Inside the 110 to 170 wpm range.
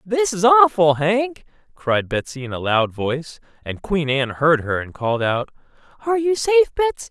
No: average, 185 wpm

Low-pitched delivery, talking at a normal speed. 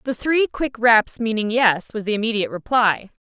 No: high, 225 Hz; average, 185 wpm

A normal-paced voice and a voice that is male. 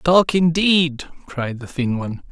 Yes: average, 155 wpm; male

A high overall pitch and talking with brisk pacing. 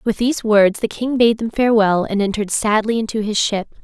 Yes: high, 220 Hz; fast, 220 wpm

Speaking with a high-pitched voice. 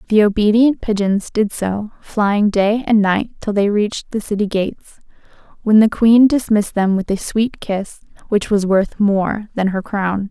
Yes: high, 205 Hz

